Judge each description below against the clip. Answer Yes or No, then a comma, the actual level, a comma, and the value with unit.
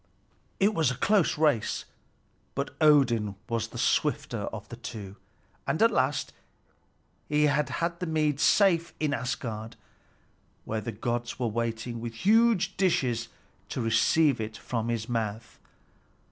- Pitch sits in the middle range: No, low, 125 Hz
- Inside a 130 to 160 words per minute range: Yes, slow, 135 wpm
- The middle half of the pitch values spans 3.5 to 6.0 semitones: Yes, average, 5.3 semitones